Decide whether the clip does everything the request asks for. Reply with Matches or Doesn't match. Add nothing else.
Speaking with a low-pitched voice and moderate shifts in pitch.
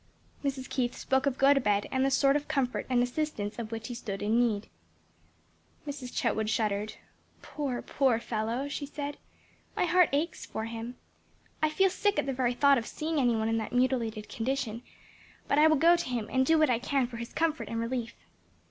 Doesn't match